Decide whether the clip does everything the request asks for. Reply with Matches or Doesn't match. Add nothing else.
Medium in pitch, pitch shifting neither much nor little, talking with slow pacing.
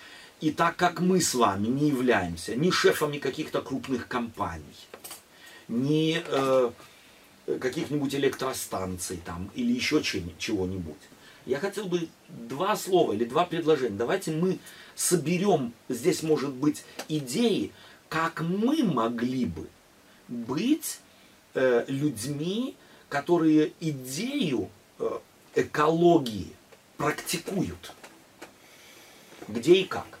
Doesn't match